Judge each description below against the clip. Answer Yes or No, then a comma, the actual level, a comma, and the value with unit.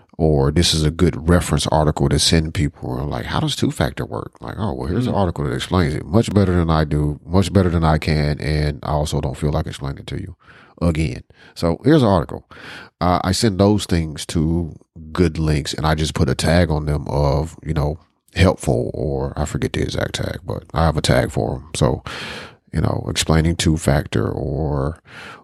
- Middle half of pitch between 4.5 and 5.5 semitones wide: No, average, 2.8 semitones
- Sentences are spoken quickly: Yes, fast, 215 wpm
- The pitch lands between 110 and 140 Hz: No, very low, 80 Hz